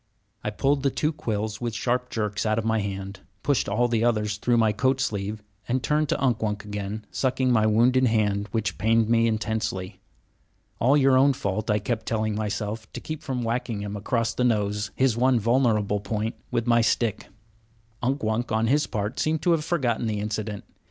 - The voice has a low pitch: Yes, low, 110 Hz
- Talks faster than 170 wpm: Yes, average, 195 wpm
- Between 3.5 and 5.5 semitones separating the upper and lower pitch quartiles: No, average, 3.0 semitones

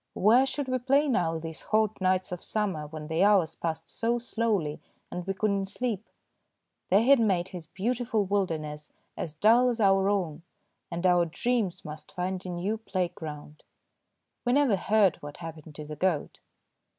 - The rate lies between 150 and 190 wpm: Yes, average, 170 wpm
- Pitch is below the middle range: No, high, 190 Hz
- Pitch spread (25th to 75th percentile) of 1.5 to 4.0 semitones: No, average, 5.2 semitones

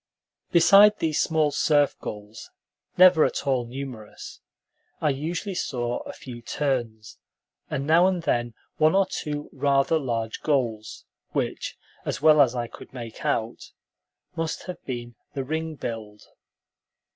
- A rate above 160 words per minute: No, slow, 135 wpm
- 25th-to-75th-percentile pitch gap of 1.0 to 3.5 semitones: No, average, 5.0 semitones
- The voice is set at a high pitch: No, medium, 140 Hz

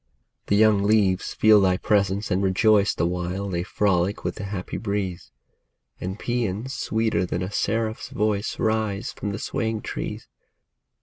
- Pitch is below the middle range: Yes, low, 100 Hz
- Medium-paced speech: Yes, average, 150 wpm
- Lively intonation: No, narrow, 2.5 semitones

